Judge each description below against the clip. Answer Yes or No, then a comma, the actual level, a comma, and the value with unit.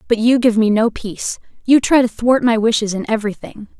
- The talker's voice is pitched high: Yes, high, 225 Hz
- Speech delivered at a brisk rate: Yes, fast, 220 wpm